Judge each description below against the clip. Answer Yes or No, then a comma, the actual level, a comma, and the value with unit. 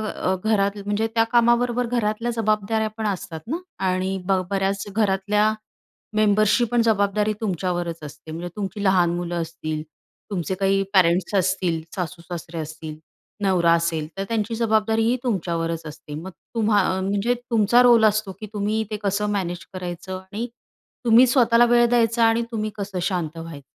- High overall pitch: Yes, high, 200 Hz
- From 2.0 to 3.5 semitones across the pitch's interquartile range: No, average, 3.9 semitones